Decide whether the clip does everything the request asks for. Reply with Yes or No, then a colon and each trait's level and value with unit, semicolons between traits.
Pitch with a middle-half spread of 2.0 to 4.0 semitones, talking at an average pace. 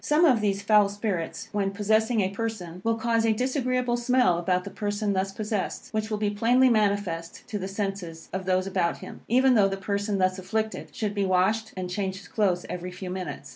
No: average, 2.9 semitones; fast, 210 wpm